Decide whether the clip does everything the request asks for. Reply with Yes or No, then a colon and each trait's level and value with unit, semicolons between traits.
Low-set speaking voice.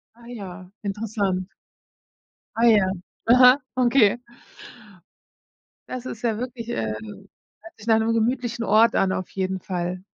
No: high, 220 Hz